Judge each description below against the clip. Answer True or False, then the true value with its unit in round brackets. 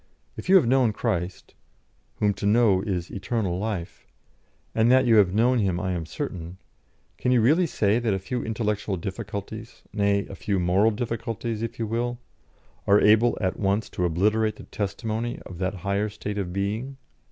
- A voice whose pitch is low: True (105 Hz)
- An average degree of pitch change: True (3.0 semitones)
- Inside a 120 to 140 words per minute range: False (175 wpm)